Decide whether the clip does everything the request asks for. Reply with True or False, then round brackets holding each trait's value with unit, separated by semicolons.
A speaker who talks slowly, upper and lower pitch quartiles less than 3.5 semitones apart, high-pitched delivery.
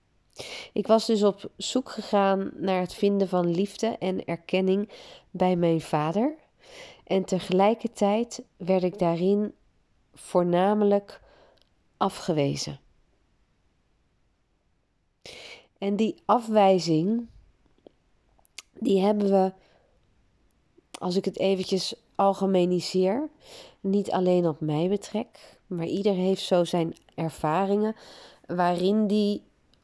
True (95 wpm; 2.9 semitones; 195 Hz)